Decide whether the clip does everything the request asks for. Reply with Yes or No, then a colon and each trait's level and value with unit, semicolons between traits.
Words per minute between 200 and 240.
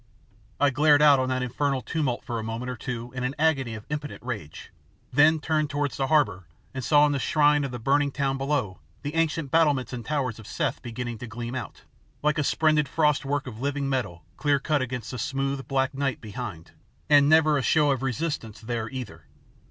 Yes: fast, 205 wpm